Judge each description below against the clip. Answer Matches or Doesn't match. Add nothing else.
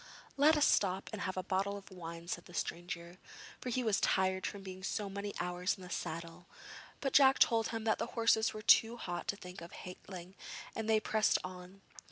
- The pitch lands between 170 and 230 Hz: Matches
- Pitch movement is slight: Doesn't match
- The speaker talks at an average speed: Doesn't match